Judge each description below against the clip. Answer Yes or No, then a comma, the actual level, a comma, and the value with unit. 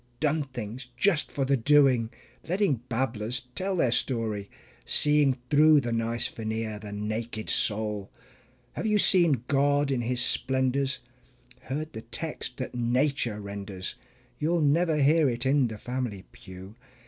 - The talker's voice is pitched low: Yes, low, 125 Hz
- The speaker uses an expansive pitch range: No, average, 4.7 semitones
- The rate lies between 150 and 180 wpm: No, average, 140 wpm